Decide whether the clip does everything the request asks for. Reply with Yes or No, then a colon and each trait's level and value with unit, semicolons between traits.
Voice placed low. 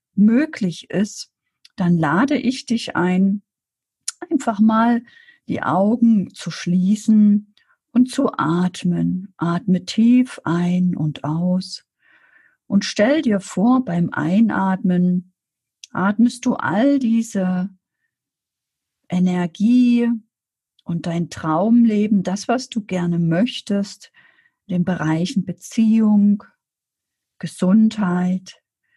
No: high, 200 Hz